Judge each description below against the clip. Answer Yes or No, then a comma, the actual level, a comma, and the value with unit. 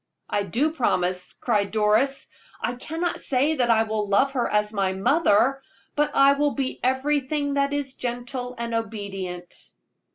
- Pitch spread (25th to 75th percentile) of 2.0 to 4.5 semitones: No, average, 5.0 semitones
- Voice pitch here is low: No, high, 245 Hz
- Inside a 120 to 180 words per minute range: Yes, average, 155 wpm